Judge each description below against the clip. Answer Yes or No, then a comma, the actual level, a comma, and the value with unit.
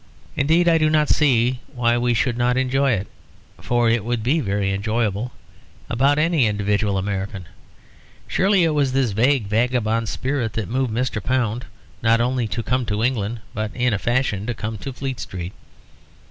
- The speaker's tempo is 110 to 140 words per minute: No, average, 175 wpm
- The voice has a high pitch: No, low, 120 Hz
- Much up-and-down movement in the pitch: No, average, 3.5 semitones